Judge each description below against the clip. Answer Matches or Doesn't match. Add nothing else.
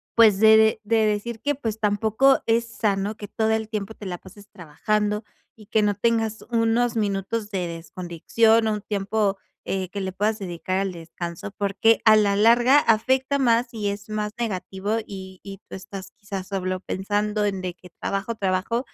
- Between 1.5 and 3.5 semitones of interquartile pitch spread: Matches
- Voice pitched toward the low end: Doesn't match